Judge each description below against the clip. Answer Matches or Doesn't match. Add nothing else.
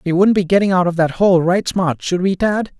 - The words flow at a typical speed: Doesn't match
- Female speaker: Doesn't match